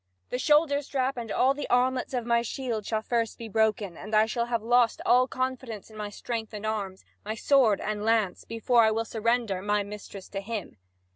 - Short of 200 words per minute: No, fast, 205 wpm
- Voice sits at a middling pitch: No, high, 225 Hz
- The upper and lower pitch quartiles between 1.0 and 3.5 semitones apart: Yes, average, 2.7 semitones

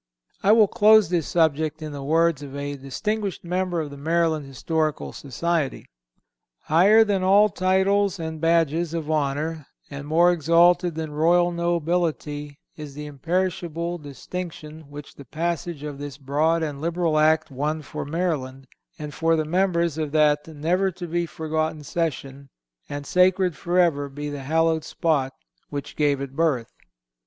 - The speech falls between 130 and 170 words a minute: Yes, average, 150 wpm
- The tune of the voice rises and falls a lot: No, average, 2.9 semitones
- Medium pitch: Yes, medium, 160 Hz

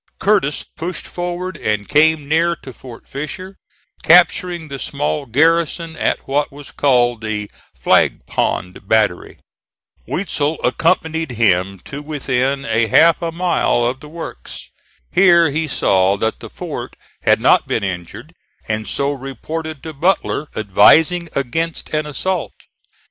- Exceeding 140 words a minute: No, slow, 135 wpm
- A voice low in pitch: No, medium, 145 Hz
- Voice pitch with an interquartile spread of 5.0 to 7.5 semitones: Yes, wide, 5.6 semitones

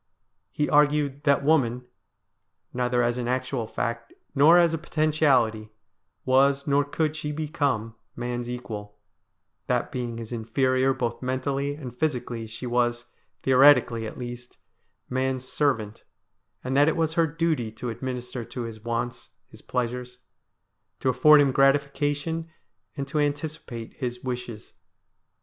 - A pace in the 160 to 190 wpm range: No, slow, 135 wpm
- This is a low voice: Yes, low, 130 Hz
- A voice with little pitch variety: No, average, 3.3 semitones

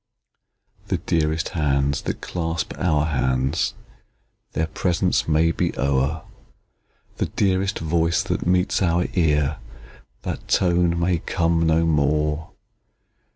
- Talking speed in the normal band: No, slow, 110 wpm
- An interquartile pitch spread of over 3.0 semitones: No, narrow, 2.4 semitones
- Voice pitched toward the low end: Yes, very low, 80 Hz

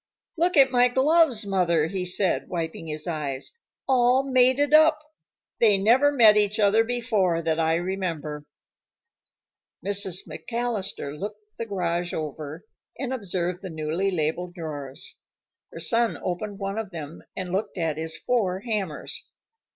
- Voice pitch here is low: No, high, 195 Hz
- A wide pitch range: Yes, wide, 6.0 semitones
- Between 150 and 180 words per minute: No, average, 140 wpm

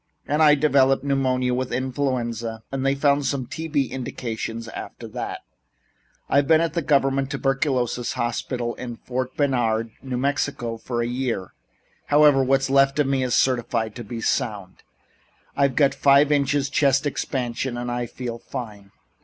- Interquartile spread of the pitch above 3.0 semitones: No, average, 2.7 semitones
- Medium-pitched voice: No, low, 130 Hz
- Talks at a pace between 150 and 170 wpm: Yes, average, 155 wpm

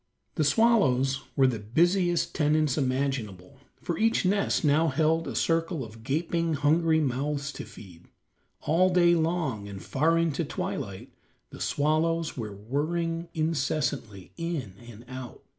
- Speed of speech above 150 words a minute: No, slow, 135 wpm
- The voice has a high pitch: No, medium, 150 Hz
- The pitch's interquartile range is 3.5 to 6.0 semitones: Yes, average, 4.5 semitones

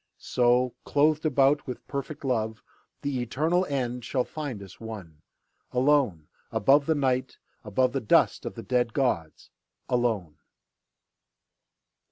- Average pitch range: Yes, average, 4.0 semitones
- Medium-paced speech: No, slow, 125 wpm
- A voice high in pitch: No, low, 125 Hz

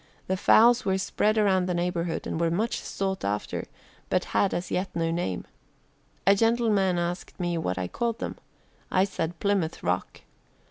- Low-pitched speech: No, medium, 185 Hz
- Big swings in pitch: No, average, 3.1 semitones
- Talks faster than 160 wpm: Yes, average, 170 wpm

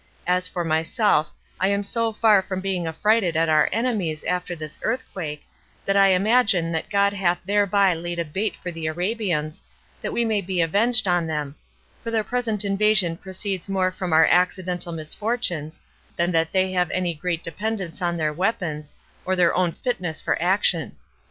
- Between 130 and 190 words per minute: Yes, average, 175 wpm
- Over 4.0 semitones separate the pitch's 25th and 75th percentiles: No, average, 3.6 semitones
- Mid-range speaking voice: Yes, medium, 180 Hz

